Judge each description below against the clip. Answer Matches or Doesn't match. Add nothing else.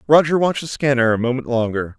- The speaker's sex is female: Doesn't match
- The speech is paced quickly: Matches